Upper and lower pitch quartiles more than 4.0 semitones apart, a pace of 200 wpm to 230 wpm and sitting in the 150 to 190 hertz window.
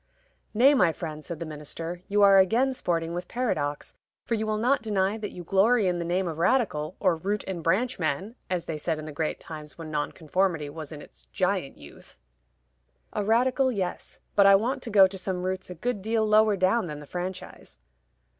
Yes: average, 4.7 semitones; fast, 205 wpm; medium, 185 Hz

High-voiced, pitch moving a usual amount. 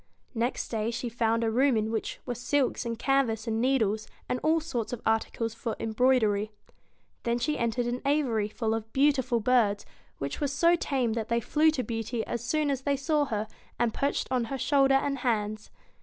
Yes: high, 240 Hz; average, 3.4 semitones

